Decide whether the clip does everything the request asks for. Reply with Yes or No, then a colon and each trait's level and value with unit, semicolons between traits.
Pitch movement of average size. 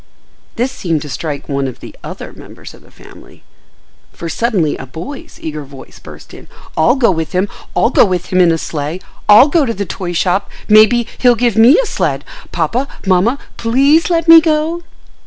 No: wide, 8.0 semitones